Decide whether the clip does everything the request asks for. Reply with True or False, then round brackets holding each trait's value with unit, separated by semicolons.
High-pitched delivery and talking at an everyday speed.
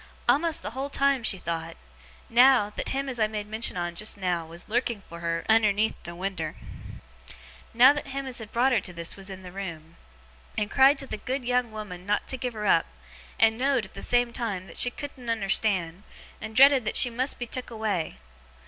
False (220 Hz; 210 wpm)